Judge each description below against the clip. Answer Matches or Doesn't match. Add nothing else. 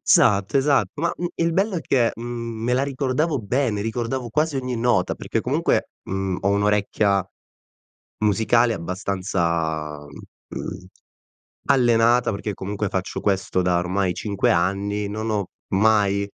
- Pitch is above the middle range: Doesn't match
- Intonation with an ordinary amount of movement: Matches